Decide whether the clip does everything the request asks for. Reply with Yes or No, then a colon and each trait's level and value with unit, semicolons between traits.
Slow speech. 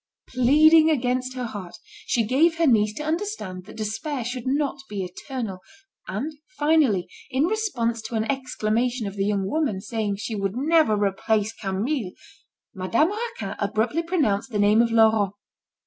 No: average, 155 wpm